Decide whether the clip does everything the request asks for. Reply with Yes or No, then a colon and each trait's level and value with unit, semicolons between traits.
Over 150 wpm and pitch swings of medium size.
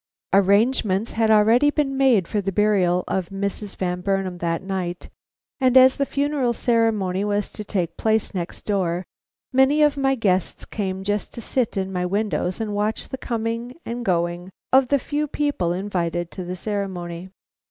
Yes: average, 170 wpm; average, 4.6 semitones